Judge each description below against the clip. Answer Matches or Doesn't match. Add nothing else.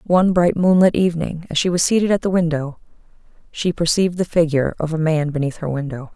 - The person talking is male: Doesn't match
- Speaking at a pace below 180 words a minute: Doesn't match